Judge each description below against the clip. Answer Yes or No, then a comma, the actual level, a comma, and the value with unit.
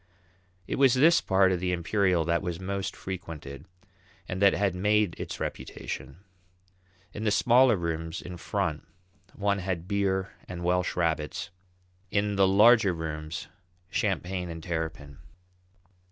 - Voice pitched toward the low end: Yes, very low, 90 Hz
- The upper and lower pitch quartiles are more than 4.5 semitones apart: No, average, 3.4 semitones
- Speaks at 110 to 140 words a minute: Yes, slow, 135 wpm